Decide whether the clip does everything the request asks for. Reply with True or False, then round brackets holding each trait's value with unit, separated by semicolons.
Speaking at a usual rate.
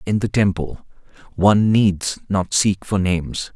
True (150 wpm)